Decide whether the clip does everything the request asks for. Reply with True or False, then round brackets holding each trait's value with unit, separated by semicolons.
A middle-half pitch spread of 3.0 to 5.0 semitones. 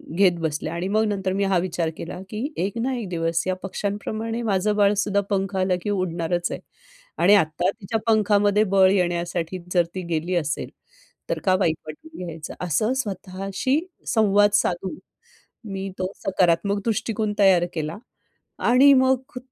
True (3.3 semitones)